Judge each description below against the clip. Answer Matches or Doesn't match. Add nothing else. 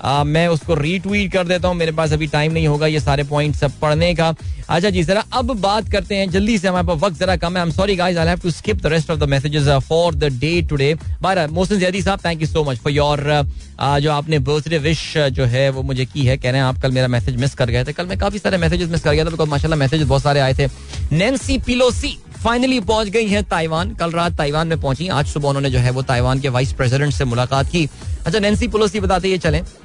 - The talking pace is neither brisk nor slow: Doesn't match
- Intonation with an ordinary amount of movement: Matches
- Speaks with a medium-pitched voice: Matches